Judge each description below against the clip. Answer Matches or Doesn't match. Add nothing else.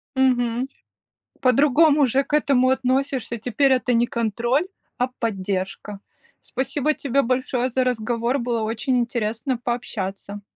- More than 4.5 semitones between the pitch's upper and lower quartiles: Doesn't match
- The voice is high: Matches